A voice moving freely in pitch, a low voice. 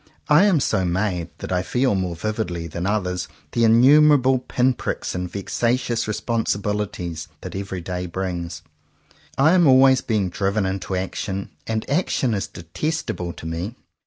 Yes: wide, 5.7 semitones; low, 100 Hz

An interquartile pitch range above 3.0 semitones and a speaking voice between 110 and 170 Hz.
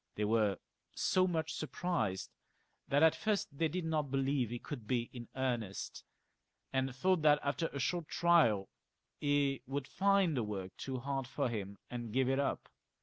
Yes: average, 5.0 semitones; low, 135 Hz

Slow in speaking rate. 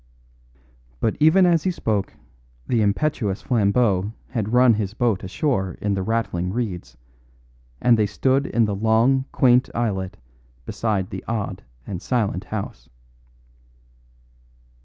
Yes: slow, 125 wpm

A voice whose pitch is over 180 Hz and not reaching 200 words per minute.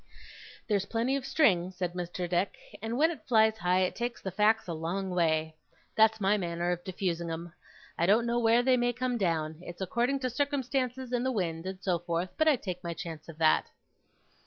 No: high, 190 Hz; fast, 205 wpm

